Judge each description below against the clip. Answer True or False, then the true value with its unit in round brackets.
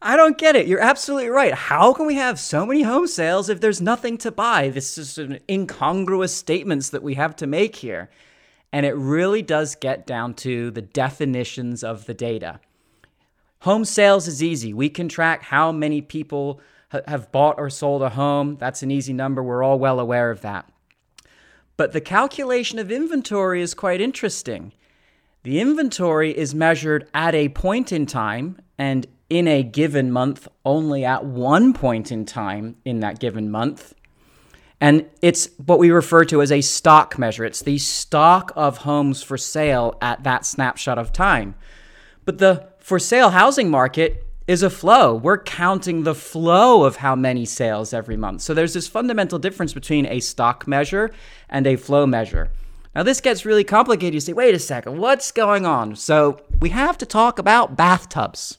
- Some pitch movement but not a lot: False (6.5 semitones)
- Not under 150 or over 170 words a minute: False (180 wpm)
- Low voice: False (150 Hz)